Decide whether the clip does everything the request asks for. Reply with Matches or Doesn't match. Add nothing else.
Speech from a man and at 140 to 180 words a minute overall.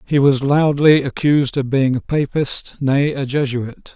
Matches